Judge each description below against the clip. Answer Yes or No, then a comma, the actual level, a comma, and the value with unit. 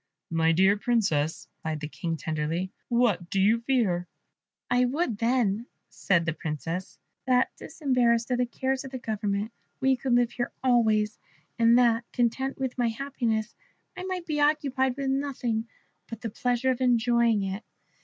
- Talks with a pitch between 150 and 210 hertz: No, high, 235 Hz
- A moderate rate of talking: Yes, average, 155 wpm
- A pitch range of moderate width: Yes, average, 4.5 semitones